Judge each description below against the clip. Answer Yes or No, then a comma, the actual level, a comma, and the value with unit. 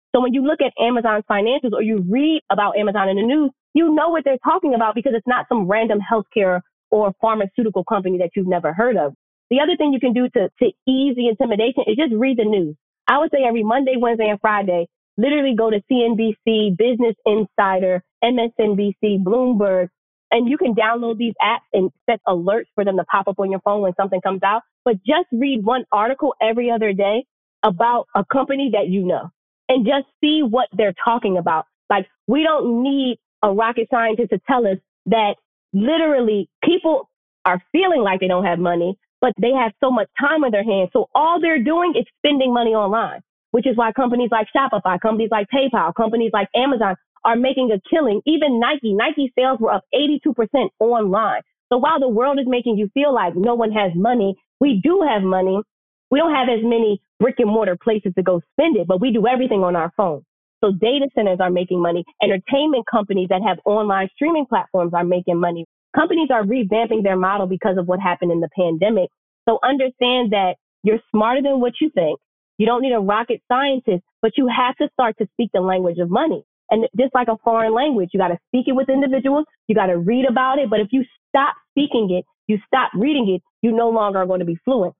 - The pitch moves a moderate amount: Yes, average, 4.7 semitones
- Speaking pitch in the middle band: No, high, 225 Hz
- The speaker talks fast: Yes, fast, 210 wpm